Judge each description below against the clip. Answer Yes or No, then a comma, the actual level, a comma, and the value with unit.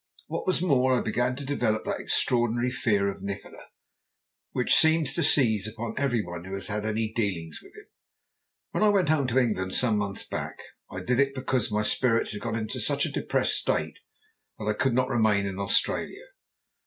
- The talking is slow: No, average, 190 wpm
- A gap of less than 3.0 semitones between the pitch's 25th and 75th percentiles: No, average, 3.8 semitones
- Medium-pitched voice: No, low, 115 Hz